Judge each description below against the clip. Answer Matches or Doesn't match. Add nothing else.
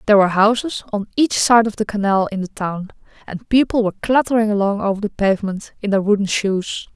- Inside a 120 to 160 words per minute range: Doesn't match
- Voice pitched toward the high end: Matches